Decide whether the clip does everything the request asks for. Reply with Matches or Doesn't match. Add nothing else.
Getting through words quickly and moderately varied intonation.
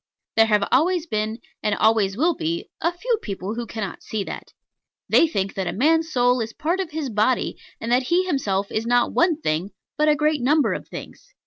Doesn't match